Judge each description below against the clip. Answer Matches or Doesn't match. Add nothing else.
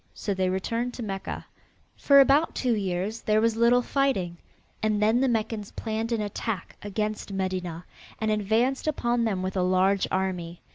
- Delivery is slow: Doesn't match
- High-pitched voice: Matches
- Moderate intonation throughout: Matches